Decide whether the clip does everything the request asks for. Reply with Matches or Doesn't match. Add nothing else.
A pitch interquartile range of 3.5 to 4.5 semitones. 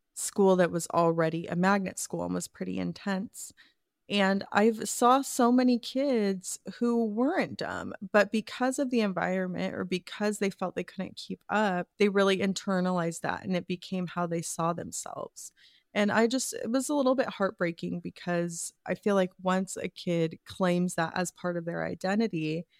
Matches